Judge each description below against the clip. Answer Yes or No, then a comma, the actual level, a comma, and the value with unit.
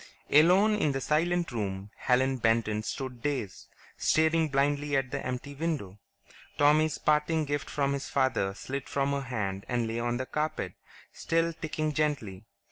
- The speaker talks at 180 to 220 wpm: No, average, 155 wpm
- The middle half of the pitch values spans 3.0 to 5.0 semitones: Yes, average, 4.3 semitones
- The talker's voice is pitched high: No, medium, 140 Hz